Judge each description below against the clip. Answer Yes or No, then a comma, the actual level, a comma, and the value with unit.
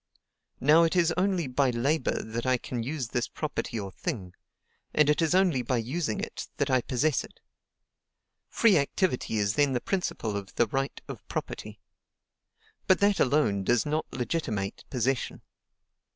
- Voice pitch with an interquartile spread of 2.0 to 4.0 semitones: No, average, 5.2 semitones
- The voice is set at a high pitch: No, low, 130 Hz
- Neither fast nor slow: Yes, average, 160 wpm